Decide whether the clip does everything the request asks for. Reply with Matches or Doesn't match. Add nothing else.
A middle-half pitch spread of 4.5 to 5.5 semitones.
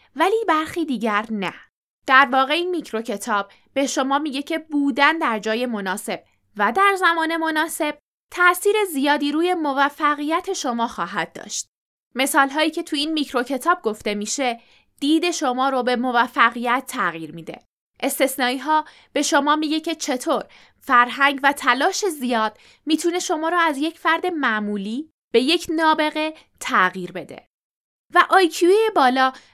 Matches